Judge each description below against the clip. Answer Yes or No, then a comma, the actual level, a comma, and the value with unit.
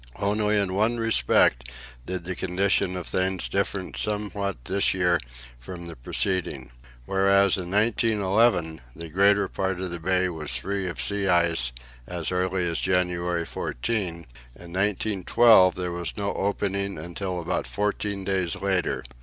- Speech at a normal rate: Yes, average, 145 wpm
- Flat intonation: Yes, narrow, 2.3 semitones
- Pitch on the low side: Yes, very low, 95 Hz